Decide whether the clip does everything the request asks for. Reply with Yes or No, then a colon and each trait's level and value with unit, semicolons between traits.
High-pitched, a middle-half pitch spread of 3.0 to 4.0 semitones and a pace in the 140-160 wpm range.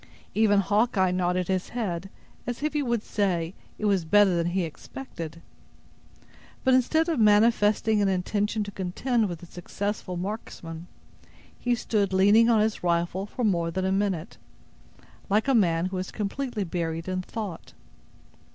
Yes: high, 200 Hz; average, 3.6 semitones; average, 155 wpm